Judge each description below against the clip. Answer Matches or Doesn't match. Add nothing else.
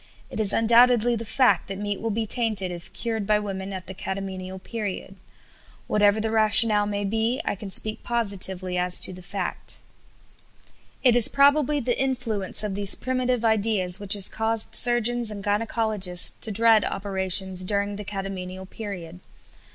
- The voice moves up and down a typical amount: Matches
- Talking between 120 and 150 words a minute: Doesn't match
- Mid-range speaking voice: Doesn't match